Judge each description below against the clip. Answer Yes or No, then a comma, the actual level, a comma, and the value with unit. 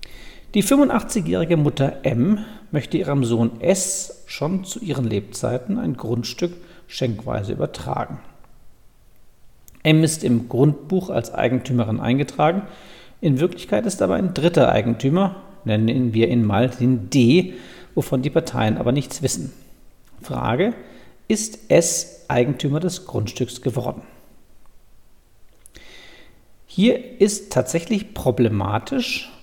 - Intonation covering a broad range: Yes, wide, 7.3 semitones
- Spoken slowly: Yes, slow, 110 wpm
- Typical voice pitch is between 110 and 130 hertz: No, medium, 140 Hz